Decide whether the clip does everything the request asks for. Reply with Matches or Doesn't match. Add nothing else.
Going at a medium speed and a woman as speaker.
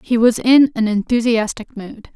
Matches